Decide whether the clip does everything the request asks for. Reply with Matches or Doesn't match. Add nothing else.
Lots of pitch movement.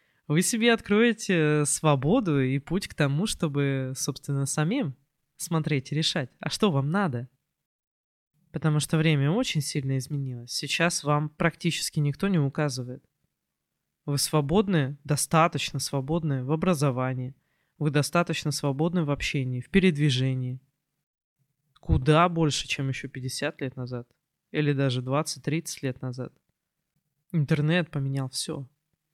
Doesn't match